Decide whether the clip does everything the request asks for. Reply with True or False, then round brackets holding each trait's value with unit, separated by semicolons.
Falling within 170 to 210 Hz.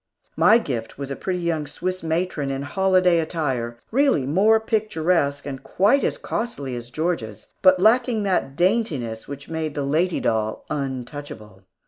False (160 Hz)